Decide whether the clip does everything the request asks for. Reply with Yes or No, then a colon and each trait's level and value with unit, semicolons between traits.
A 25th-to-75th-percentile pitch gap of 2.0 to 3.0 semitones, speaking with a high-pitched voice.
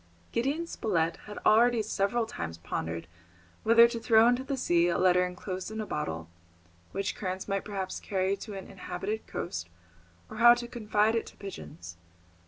No: average, 4.2 semitones; high, 200 Hz